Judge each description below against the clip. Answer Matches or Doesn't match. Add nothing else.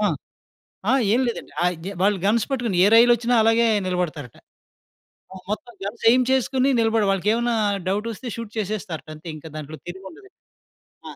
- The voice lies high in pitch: Matches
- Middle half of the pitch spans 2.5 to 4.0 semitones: Doesn't match